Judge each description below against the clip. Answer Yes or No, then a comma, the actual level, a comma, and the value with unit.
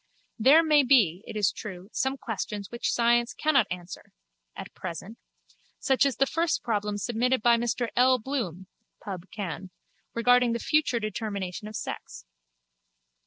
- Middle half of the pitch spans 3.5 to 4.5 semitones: Yes, average, 4.2 semitones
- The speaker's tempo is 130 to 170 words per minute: Yes, slow, 135 wpm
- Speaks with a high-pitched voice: Yes, high, 230 Hz